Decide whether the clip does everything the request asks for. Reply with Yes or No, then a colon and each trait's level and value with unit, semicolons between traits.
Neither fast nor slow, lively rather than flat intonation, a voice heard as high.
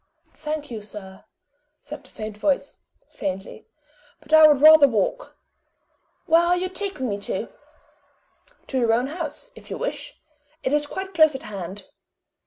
Yes: average, 155 wpm; wide, 6.8 semitones; very high, 290 Hz